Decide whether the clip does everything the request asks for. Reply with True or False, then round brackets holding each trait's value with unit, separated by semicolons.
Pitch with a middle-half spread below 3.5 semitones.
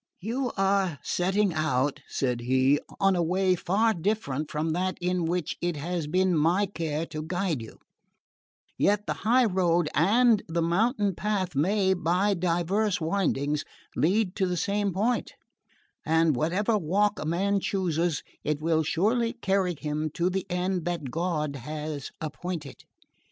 False (4.0 semitones)